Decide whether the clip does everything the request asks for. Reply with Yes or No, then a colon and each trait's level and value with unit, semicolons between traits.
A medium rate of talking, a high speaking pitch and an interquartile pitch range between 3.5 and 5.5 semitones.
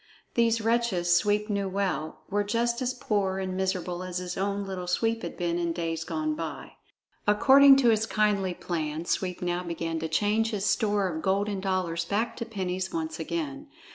Yes: average, 180 wpm; high, 195 Hz; average, 4.0 semitones